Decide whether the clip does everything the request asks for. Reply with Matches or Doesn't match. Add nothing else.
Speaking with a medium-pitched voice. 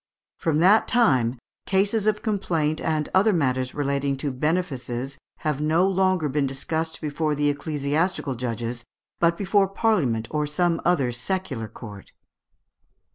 Matches